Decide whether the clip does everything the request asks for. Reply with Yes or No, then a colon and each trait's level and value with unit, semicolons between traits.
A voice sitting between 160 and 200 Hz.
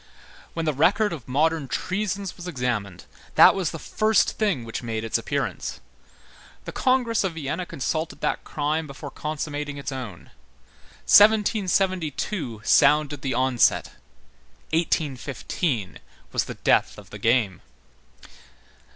No: medium, 150 Hz